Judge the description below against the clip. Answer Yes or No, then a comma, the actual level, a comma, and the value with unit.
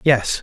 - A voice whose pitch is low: Yes, low, 125 Hz